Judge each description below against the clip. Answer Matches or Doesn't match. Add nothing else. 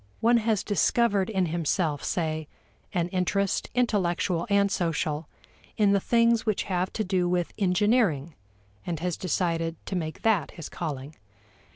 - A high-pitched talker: Doesn't match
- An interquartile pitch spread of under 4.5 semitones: Matches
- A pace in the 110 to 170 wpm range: Matches